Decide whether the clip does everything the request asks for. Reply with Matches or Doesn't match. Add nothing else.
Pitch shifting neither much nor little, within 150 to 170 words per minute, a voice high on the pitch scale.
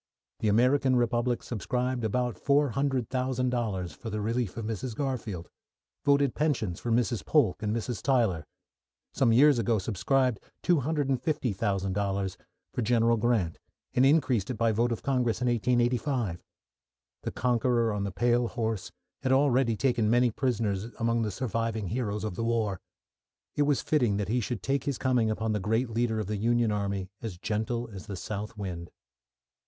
Doesn't match